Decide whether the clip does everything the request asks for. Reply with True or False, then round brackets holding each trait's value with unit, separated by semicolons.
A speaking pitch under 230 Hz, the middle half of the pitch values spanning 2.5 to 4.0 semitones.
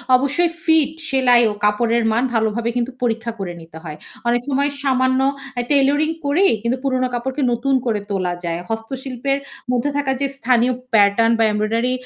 False (245 Hz; 3.2 semitones)